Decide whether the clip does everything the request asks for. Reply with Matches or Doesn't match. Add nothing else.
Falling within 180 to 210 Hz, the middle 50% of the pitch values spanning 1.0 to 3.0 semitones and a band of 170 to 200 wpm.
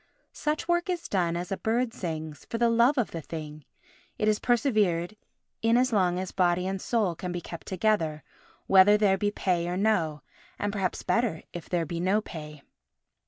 Doesn't match